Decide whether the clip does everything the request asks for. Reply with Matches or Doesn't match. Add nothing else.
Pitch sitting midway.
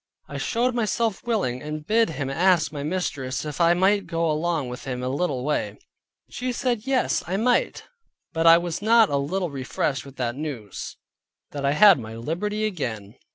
Matches